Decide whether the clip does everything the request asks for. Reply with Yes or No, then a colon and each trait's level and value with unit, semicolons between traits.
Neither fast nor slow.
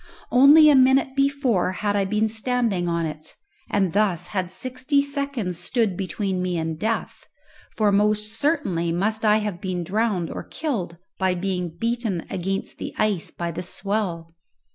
Yes: average, 160 wpm